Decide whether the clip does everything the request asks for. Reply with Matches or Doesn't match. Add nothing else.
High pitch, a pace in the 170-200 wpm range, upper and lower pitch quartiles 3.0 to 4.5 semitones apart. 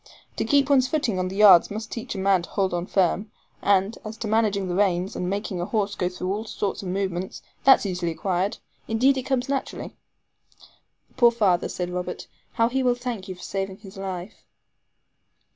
Matches